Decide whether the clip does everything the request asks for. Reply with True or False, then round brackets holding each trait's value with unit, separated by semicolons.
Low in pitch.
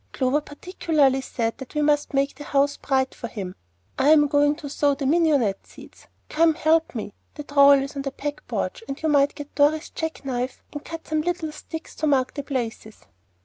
False (285 Hz)